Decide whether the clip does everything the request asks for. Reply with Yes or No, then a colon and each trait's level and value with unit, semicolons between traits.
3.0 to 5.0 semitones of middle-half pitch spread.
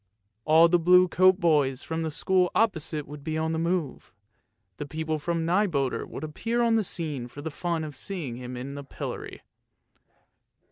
Yes: average, 3.7 semitones